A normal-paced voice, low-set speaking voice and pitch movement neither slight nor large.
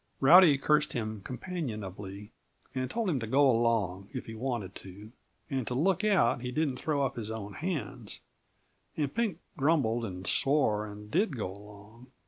No: average, 165 wpm; low, 125 Hz; wide, 5.9 semitones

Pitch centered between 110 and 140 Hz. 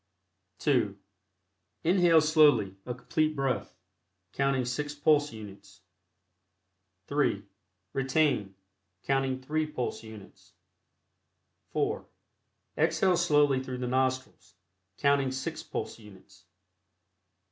Yes: low, 135 Hz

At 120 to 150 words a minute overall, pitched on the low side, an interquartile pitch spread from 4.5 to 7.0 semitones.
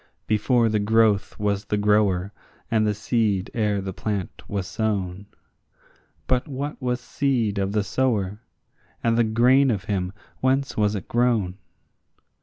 No: average, 145 wpm; low, 105 Hz; average, 3.0 semitones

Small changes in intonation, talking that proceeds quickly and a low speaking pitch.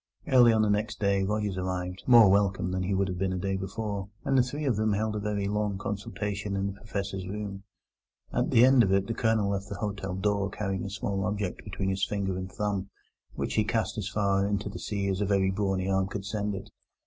Yes: narrow, 1.5 semitones; fast, 235 wpm; low, 100 Hz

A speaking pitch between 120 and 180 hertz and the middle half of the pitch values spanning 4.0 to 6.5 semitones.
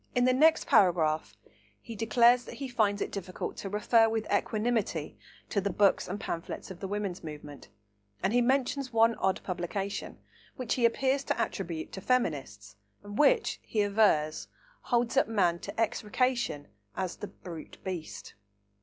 No: high, 205 Hz; average, 5.2 semitones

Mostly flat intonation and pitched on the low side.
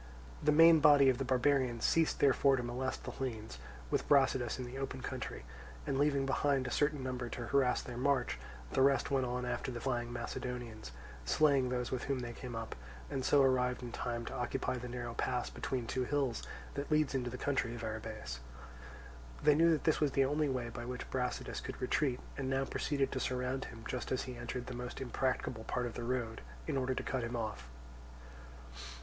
Yes: narrow, 2.1 semitones; low, 125 Hz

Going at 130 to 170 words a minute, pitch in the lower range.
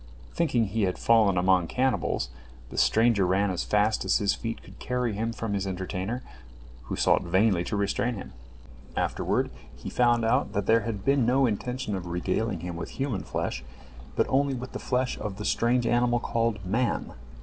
No: average, 180 wpm; low, 110 Hz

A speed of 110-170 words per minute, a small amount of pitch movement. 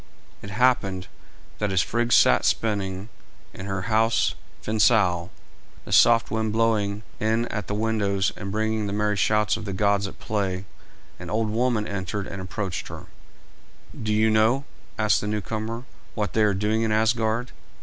Yes: average, 160 wpm; narrow, 2.0 semitones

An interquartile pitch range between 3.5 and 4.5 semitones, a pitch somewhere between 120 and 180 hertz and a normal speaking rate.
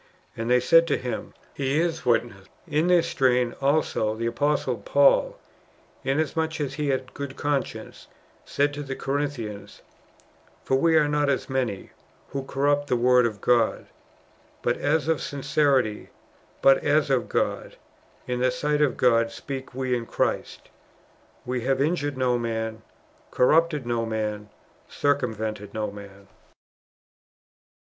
Yes: average, 3.9 semitones; low, 135 Hz; average, 145 wpm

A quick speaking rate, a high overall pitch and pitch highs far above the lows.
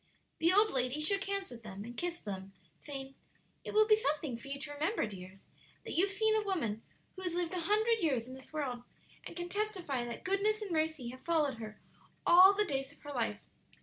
Yes: fast, 215 wpm; very high, 310 Hz; wide, 7.8 semitones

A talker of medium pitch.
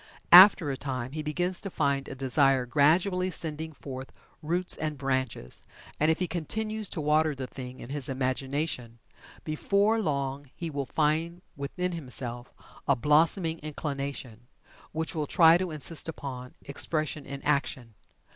Yes: medium, 150 Hz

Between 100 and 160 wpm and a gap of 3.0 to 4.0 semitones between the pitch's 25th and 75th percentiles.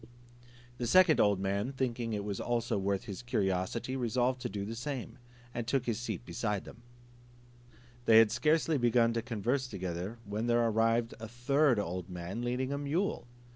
No: average, 170 wpm; average, 3.6 semitones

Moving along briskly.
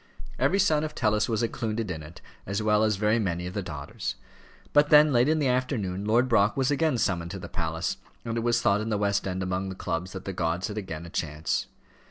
Yes: fast, 240 wpm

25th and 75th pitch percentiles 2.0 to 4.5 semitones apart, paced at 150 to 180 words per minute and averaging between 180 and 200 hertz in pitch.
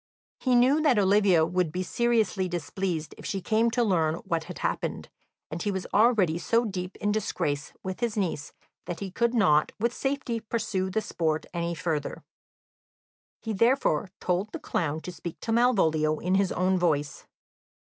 No: average, 5.1 semitones; average, 170 wpm; high, 190 Hz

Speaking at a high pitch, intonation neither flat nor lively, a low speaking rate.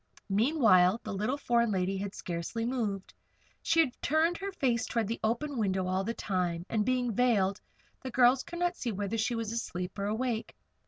No: high, 225 Hz; average, 4.5 semitones; average, 190 wpm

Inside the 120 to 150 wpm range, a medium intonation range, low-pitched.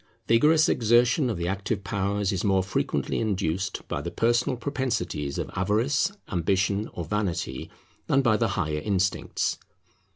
Yes: average, 140 wpm; average, 4.1 semitones; low, 100 Hz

